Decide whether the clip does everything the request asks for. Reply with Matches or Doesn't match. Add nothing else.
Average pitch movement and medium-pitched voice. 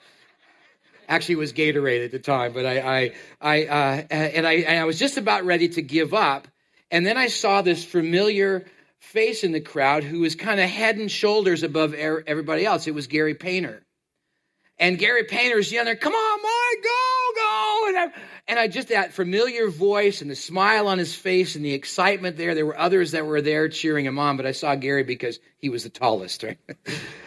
Doesn't match